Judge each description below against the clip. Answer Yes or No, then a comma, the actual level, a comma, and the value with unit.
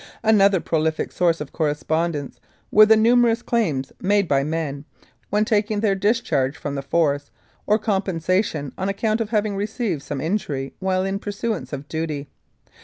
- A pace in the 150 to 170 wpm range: Yes, average, 160 wpm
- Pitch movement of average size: No, wide, 6.0 semitones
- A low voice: No, medium, 185 Hz